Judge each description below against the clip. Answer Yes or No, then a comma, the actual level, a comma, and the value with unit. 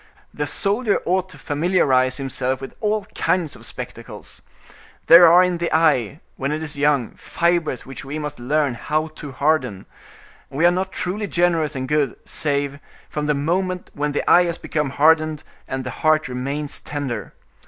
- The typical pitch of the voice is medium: Yes, medium, 150 Hz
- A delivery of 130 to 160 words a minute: No, average, 175 wpm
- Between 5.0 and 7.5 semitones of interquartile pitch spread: No, average, 3.8 semitones